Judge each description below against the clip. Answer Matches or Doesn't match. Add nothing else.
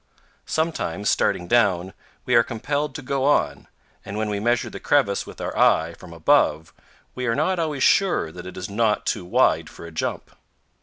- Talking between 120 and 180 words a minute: Doesn't match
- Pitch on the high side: Doesn't match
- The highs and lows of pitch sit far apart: Matches